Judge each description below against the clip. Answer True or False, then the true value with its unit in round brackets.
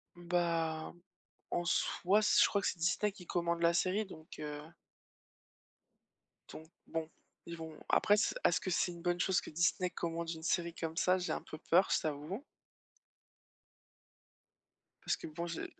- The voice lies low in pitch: False (170 Hz)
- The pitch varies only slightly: True (1.8 semitones)